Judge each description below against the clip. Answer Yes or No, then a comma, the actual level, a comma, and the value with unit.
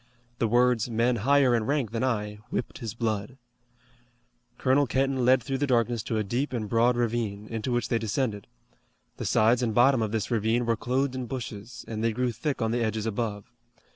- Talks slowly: No, average, 200 wpm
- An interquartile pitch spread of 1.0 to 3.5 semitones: Yes, narrow, 2.4 semitones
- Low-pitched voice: Yes, low, 120 Hz